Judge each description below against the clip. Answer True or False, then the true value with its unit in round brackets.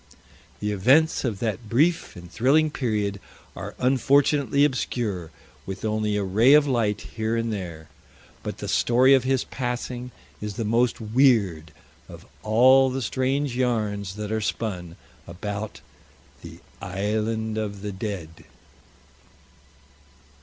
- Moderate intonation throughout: True (4.0 semitones)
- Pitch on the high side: False (110 Hz)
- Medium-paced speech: False (130 wpm)